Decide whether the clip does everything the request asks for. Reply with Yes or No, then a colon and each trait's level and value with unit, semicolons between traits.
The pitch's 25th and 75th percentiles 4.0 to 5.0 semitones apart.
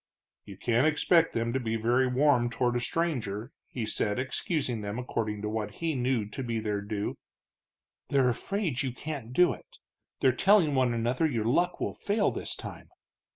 Yes: average, 4.5 semitones